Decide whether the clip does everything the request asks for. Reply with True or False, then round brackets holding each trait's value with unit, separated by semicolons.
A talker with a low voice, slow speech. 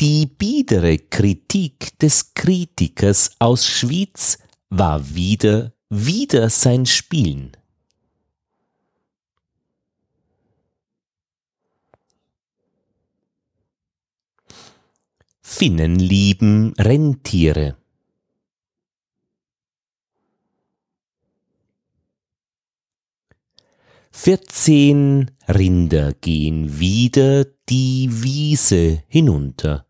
True (115 Hz; 45 wpm)